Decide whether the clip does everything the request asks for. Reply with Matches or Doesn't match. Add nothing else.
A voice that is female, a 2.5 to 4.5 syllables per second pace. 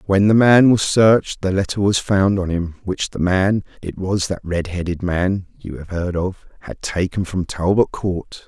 Doesn't match